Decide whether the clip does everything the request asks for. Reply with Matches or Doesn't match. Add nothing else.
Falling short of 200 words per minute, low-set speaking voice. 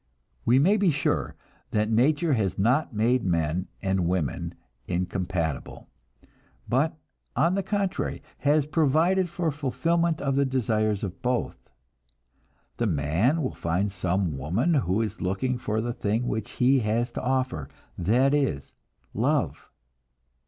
Matches